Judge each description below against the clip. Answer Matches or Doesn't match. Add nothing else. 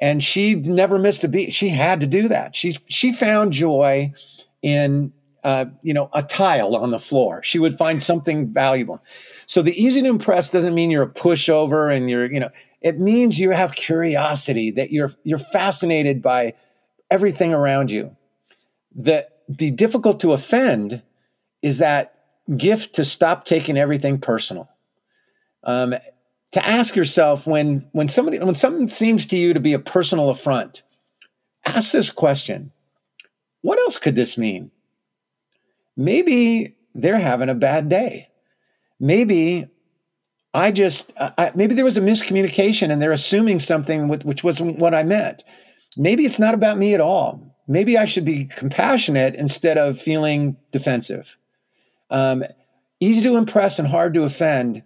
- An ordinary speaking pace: Matches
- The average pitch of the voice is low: Doesn't match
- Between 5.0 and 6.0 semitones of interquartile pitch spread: Matches